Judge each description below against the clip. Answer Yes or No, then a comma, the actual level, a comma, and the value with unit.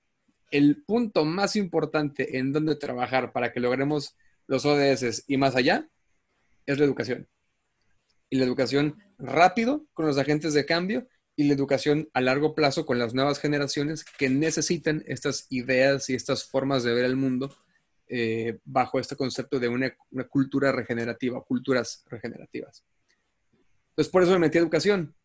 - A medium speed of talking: Yes, average, 160 wpm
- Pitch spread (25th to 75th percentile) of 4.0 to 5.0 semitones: No, average, 3.2 semitones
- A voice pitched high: No, medium, 140 Hz